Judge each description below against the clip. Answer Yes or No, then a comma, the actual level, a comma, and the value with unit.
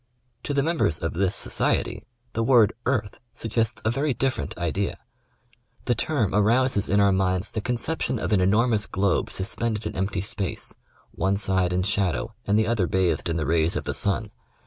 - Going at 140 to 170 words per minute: No, average, 190 wpm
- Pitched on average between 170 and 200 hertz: No, low, 100 Hz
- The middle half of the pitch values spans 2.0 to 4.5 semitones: Yes, average, 3.8 semitones